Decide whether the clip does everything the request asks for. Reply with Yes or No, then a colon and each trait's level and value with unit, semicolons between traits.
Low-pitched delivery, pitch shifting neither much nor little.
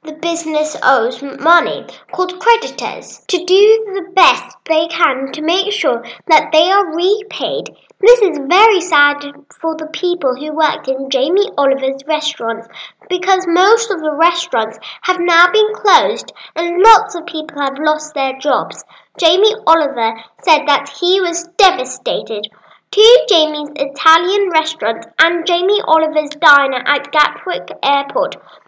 No: very high, 320 Hz; average, 4.5 semitones